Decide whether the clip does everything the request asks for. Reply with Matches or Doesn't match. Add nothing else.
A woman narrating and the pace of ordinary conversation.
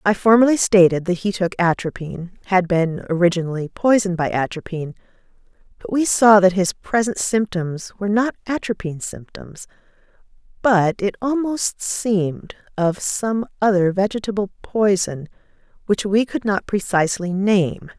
Doesn't match